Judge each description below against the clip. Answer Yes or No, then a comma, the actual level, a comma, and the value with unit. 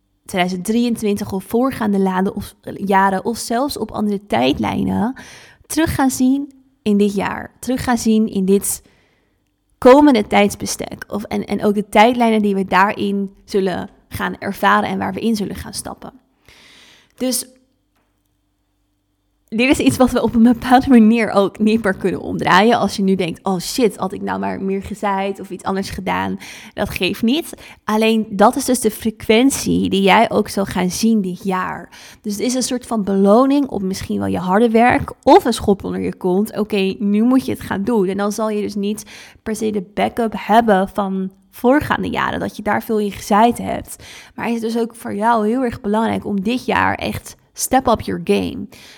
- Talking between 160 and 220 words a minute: Yes, average, 190 wpm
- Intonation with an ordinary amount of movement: Yes, average, 3.3 semitones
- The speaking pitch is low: No, high, 210 Hz